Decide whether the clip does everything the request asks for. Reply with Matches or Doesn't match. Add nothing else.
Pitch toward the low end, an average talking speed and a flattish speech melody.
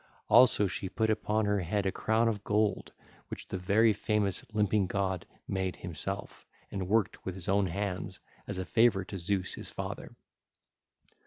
Matches